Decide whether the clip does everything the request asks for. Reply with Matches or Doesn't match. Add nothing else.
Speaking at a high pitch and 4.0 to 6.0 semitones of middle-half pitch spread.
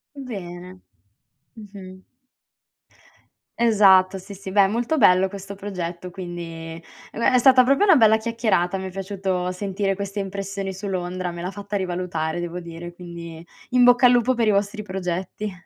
Doesn't match